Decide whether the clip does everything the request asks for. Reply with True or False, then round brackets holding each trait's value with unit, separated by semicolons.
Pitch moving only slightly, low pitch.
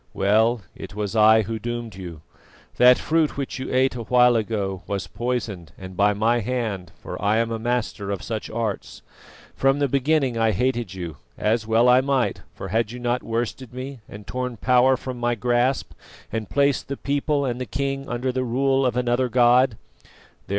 False (3.0 semitones; 120 Hz)